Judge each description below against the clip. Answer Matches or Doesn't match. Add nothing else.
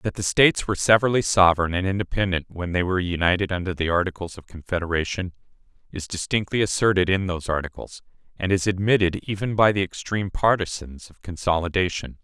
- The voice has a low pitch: Matches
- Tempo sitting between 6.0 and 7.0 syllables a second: Matches